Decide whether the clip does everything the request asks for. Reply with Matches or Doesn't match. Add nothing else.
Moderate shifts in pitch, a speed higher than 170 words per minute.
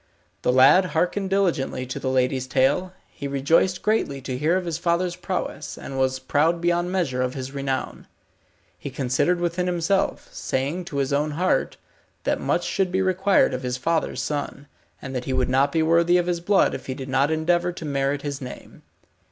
Matches